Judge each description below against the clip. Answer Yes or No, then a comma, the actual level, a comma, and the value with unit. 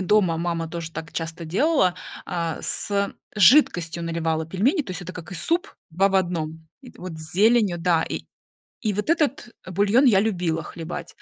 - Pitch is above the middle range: No, medium, 180 Hz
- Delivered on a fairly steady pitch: No, average, 4.1 semitones